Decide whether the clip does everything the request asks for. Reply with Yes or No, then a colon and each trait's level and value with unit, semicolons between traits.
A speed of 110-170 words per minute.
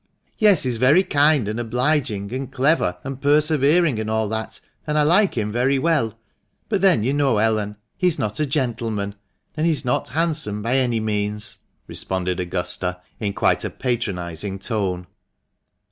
Yes: average, 165 wpm